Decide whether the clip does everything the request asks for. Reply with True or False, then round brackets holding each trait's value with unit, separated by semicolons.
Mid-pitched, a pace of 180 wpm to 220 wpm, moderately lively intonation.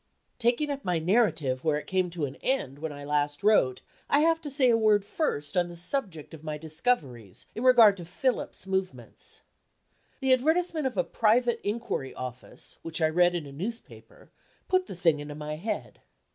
False (180 Hz; 185 wpm; 8.3 semitones)